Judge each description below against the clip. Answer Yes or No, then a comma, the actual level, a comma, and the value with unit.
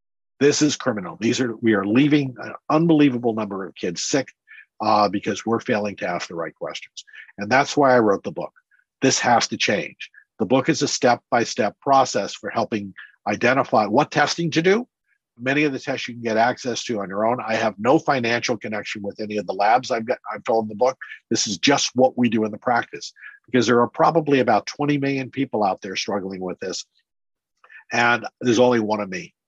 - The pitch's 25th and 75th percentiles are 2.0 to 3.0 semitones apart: No, average, 4.4 semitones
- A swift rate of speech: Yes, fast, 210 wpm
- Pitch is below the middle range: Yes, low, 120 Hz